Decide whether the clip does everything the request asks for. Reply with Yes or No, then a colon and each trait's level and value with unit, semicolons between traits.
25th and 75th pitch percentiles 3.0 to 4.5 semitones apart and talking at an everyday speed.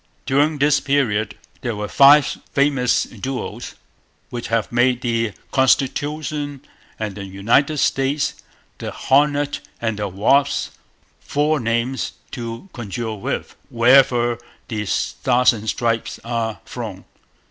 No: average, 3.8 semitones; slow, 115 wpm